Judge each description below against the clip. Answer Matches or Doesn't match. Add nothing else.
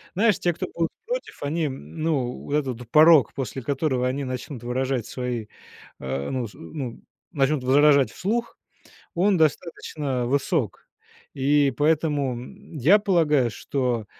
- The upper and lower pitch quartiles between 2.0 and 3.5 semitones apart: Doesn't match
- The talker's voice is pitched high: Doesn't match